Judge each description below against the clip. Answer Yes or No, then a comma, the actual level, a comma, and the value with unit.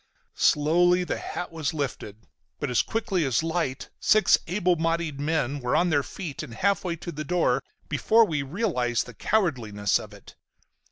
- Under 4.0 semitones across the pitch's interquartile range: No, average, 4.8 semitones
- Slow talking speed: No, average, 170 wpm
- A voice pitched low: No, medium, 160 Hz